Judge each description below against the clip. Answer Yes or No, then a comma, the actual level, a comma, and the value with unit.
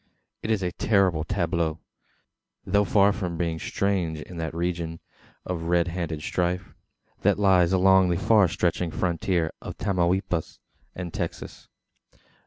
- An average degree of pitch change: No, narrow, 2.2 semitones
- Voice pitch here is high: No, very low, 90 Hz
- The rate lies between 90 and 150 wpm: Yes, slow, 135 wpm